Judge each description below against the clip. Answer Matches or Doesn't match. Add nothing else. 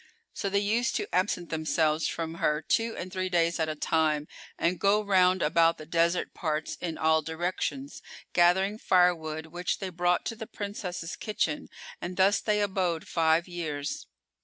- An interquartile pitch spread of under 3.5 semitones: Matches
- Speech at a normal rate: Matches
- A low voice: Doesn't match